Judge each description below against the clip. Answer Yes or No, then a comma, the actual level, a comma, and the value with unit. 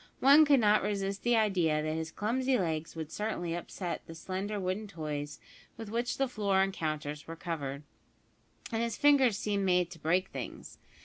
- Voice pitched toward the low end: No, high, 190 Hz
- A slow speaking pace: No, average, 180 wpm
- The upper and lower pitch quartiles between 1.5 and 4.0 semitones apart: No, average, 5.1 semitones